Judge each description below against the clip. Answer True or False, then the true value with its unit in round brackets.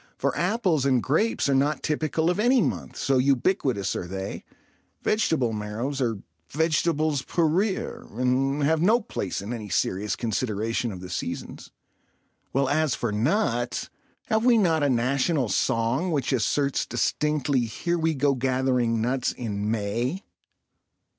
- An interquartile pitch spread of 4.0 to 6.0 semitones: True (5.5 semitones)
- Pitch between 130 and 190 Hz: True (135 Hz)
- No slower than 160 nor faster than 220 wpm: False (145 wpm)